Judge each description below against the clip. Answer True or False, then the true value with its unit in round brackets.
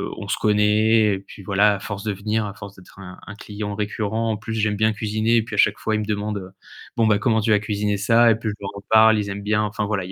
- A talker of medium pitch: False (105 Hz)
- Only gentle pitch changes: True (1.3 semitones)